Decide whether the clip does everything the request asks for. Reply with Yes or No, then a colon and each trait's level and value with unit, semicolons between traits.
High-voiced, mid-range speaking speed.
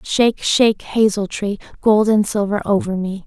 Yes: high, 205 Hz; average, 165 wpm